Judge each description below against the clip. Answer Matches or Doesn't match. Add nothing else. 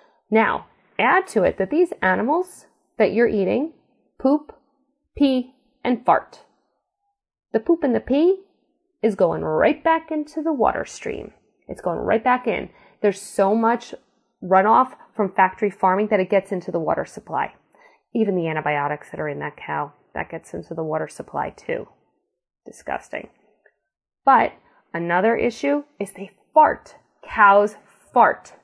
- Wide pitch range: Matches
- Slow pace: Doesn't match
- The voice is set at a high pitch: Matches